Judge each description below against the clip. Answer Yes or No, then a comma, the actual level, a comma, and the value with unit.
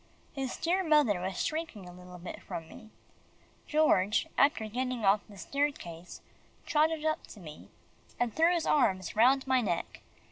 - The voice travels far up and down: Yes, wide, 8.2 semitones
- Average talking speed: Yes, average, 155 wpm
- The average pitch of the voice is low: No, high, 245 Hz